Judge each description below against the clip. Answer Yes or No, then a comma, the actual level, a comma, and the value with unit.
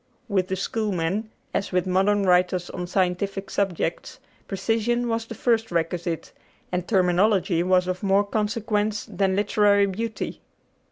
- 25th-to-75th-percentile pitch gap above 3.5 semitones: No, narrow, 2.6 semitones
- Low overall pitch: No, high, 195 Hz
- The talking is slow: Yes, slow, 130 wpm